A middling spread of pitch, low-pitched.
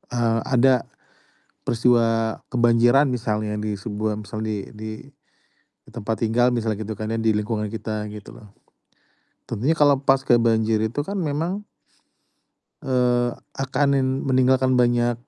Yes: average, 3.0 semitones; low, 115 Hz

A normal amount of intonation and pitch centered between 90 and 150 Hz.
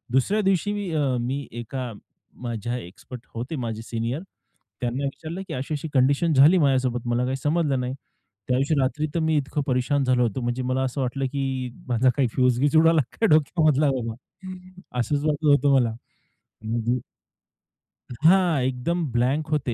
Yes: average, 3.8 semitones; low, 135 Hz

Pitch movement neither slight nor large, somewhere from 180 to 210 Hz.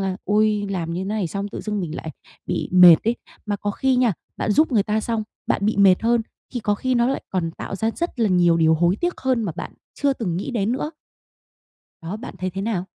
Yes: average, 4.1 semitones; high, 205 Hz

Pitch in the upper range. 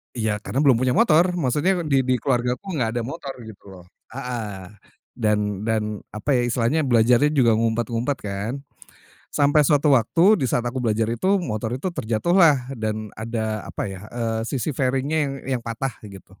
No: low, 120 Hz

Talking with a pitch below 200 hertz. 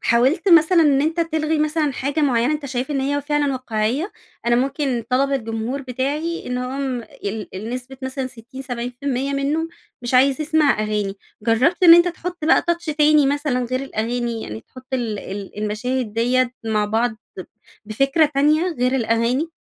No: very high, 265 Hz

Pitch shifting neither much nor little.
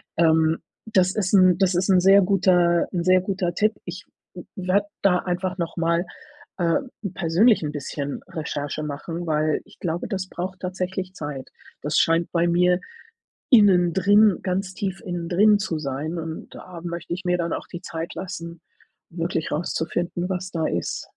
No: narrow, 2.1 semitones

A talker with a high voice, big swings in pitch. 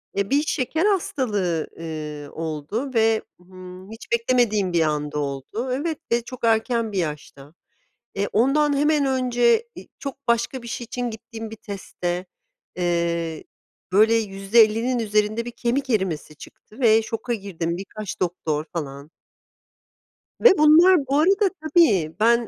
Yes: high, 220 Hz; wide, 6.3 semitones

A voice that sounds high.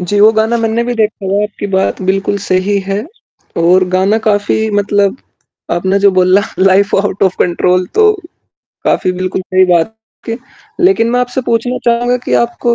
Yes: high, 205 Hz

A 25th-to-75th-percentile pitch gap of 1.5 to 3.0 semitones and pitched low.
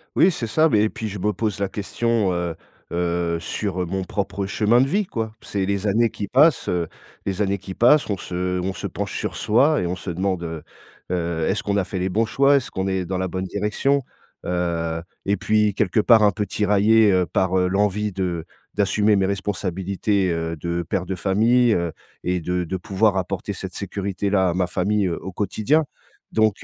Yes: average, 2.7 semitones; very low, 95 Hz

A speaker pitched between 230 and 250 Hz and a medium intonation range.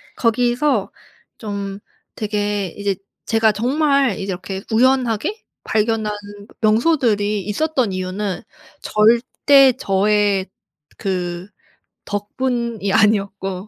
No: high, 210 Hz; average, 3.4 semitones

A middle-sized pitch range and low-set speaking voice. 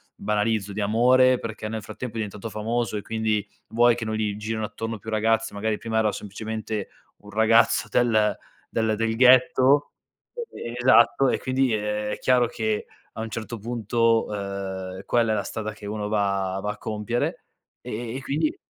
No: narrow, 1.9 semitones; low, 110 Hz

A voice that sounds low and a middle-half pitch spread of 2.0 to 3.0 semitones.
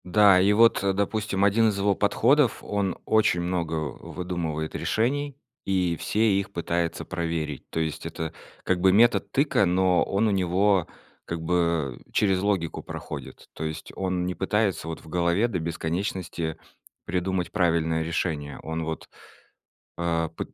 No: very low, 90 Hz; average, 3.5 semitones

